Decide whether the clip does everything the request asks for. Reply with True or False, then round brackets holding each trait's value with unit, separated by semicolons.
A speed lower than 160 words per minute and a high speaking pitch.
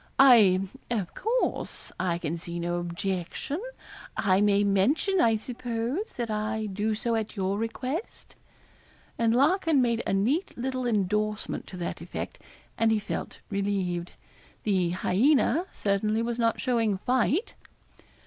True (135 wpm; 220 Hz)